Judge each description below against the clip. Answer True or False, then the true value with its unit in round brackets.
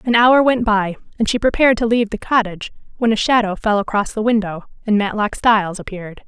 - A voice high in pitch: True (215 Hz)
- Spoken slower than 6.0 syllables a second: False (6.1 syllables/s)